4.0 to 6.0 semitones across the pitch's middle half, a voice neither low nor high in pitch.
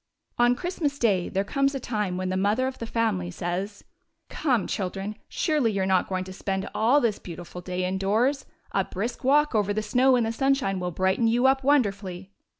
No: average, 5.3 semitones; high, 210 Hz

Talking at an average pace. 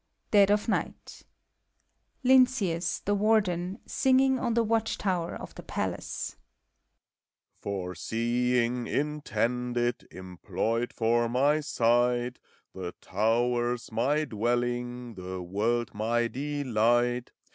No: slow, 100 wpm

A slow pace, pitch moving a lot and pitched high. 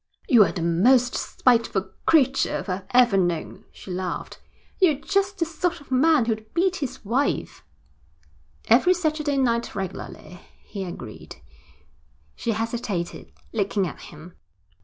Yes: slow, 130 wpm; wide, 7.3 semitones; high, 235 Hz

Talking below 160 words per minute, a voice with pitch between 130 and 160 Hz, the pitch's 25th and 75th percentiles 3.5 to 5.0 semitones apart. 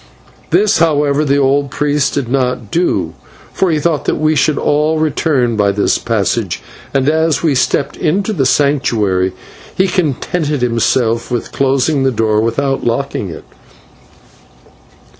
Yes: average, 140 wpm; medium, 140 Hz; average, 4.0 semitones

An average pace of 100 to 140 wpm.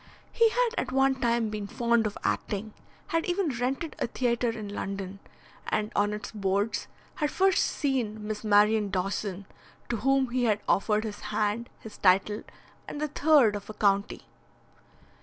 No: average, 160 wpm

